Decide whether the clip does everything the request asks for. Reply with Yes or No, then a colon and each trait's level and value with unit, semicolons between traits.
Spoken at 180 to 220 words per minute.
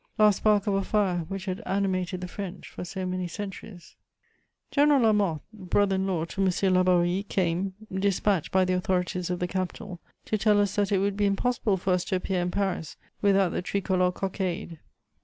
Yes: average, 190 wpm